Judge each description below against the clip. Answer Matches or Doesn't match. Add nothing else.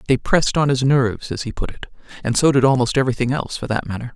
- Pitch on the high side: Doesn't match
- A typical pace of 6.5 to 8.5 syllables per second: Matches